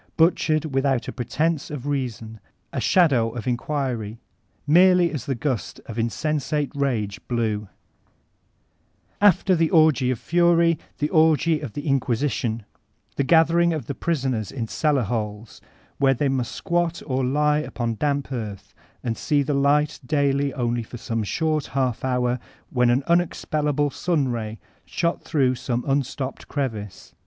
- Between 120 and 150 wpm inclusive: Yes, average, 145 wpm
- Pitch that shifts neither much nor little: Yes, average, 4.2 semitones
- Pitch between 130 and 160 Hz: Yes, low, 135 Hz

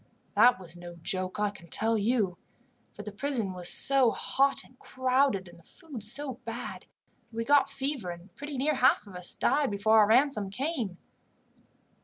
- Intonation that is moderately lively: No, wide, 6.0 semitones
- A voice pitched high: Yes, high, 225 Hz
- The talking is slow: No, average, 180 wpm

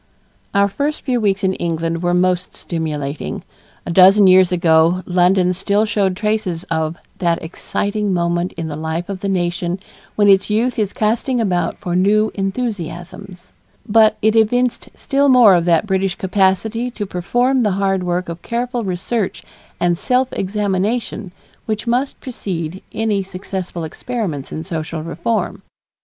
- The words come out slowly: No, average, 150 wpm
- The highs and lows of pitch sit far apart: No, average, 3.7 semitones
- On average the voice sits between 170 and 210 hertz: Yes, high, 190 Hz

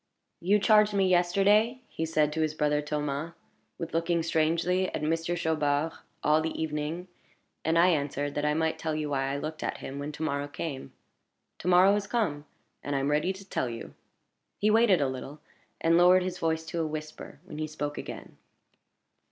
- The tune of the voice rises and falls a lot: No, average, 3.3 semitones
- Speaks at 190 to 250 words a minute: Yes, average, 195 wpm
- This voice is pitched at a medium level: Yes, medium, 160 Hz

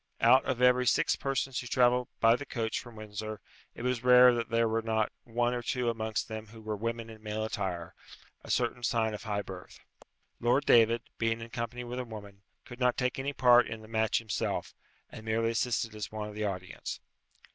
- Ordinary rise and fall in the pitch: No, narrow, 2.1 semitones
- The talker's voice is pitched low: Yes, low, 115 Hz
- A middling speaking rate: No, fast, 210 wpm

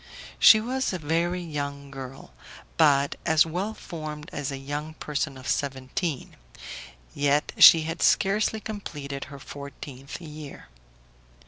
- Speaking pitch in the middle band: Yes, medium, 150 Hz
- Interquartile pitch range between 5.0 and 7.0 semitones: No, average, 3.3 semitones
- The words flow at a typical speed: No, slow, 125 wpm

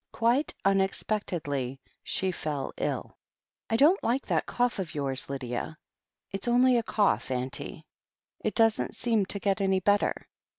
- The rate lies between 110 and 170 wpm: Yes, average, 140 wpm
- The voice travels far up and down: Yes, wide, 7.4 semitones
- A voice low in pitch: No, high, 195 Hz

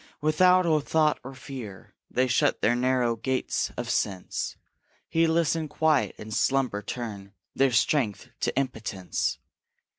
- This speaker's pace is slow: Yes, slow, 130 wpm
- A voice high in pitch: No, low, 130 Hz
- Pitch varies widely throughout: Yes, wide, 5.7 semitones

